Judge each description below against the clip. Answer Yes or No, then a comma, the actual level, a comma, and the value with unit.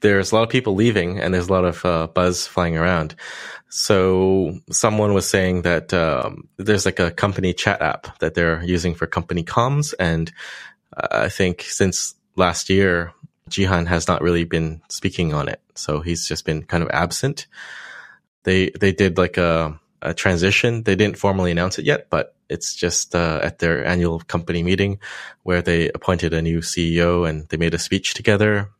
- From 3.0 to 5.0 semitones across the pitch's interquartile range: No, narrow, 2.5 semitones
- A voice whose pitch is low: Yes, very low, 90 Hz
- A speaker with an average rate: Yes, average, 185 wpm